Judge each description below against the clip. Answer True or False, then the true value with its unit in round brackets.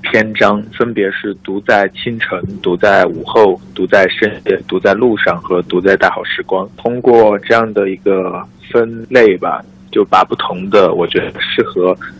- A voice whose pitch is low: True (105 Hz)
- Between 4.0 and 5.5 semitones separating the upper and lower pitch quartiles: False (3.2 semitones)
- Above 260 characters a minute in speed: False (235 characters per minute)